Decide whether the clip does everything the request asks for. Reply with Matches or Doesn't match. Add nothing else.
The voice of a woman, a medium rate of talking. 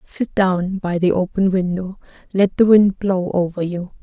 Matches